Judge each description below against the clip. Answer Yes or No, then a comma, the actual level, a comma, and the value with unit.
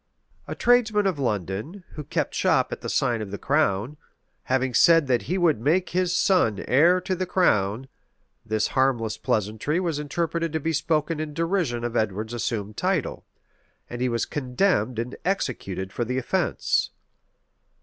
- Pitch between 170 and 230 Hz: No, low, 135 Hz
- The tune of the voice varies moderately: No, wide, 6.9 semitones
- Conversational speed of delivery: Yes, average, 160 wpm